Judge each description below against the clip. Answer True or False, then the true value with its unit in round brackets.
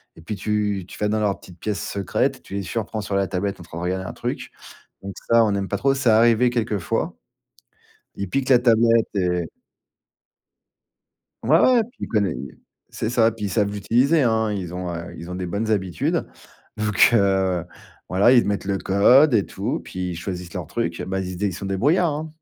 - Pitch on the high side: False (100 Hz)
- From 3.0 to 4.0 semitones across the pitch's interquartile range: True (3.5 semitones)